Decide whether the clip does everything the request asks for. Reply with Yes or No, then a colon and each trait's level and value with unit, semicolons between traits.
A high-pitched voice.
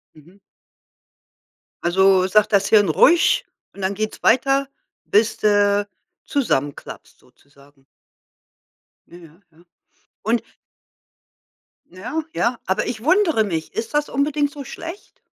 Yes: high, 210 Hz